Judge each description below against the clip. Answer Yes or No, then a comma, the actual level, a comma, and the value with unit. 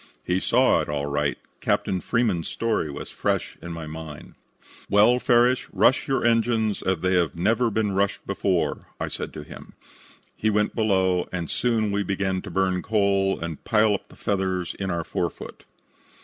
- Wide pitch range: No, average, 3.8 semitones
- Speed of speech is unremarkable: Yes, average, 175 wpm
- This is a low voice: Yes, very low, 95 Hz